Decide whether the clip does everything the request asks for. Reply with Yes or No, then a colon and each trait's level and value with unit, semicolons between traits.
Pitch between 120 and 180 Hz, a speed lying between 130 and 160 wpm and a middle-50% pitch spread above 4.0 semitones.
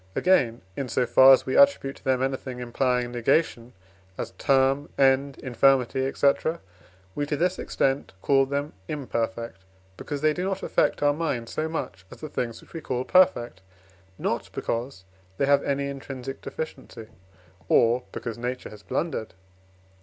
No: low, 135 Hz; average, 155 wpm; average, 3.0 semitones